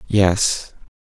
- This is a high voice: No, very low, 95 Hz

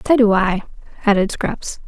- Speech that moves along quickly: No, average, 160 wpm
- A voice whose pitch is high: Yes, high, 210 Hz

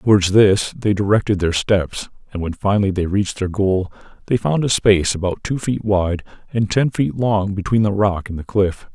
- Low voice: Yes, low, 100 Hz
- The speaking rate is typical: No, fast, 210 wpm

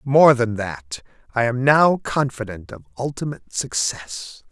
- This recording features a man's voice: Yes, male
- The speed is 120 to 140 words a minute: Yes, slow, 135 wpm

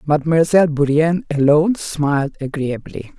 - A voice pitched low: No, medium, 150 Hz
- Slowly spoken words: Yes, slow, 95 wpm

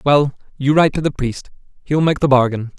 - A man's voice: Yes, male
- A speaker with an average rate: No, fast, 215 wpm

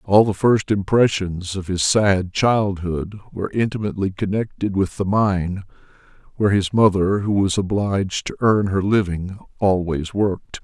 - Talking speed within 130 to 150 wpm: Yes, average, 145 wpm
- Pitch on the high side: No, low, 100 Hz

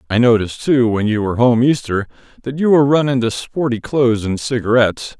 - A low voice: Yes, low, 120 Hz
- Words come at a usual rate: Yes, average, 195 wpm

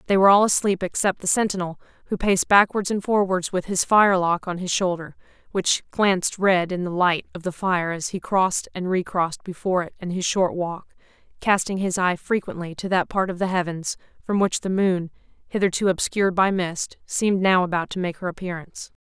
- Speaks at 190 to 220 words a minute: Yes, average, 200 wpm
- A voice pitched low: No, medium, 185 Hz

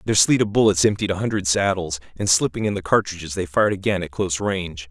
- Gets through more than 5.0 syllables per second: Yes, 6.5 syllables/s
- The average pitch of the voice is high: No, very low, 95 Hz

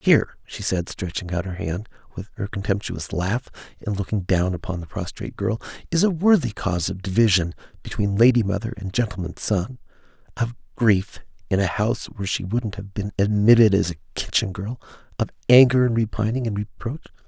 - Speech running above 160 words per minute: Yes, average, 175 wpm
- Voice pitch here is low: Yes, low, 105 Hz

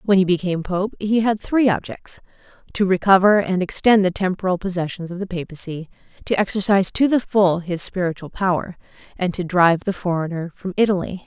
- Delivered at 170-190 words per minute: Yes, average, 175 wpm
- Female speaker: Yes, female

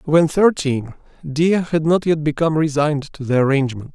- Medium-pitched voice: Yes, medium, 150 Hz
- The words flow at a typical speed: Yes, average, 165 wpm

